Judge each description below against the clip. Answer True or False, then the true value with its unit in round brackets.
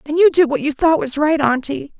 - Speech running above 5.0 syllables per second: True (5.4 syllables/s)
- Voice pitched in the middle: False (285 Hz)